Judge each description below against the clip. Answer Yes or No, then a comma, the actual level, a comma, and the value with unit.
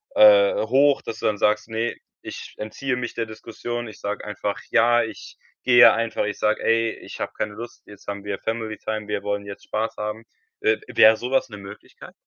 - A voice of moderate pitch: No, low, 110 Hz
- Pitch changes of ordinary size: No, narrow, 2.3 semitones